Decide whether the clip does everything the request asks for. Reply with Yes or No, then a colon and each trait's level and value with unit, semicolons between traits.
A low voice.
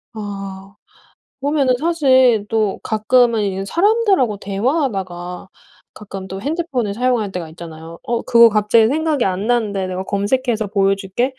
No: high, 215 Hz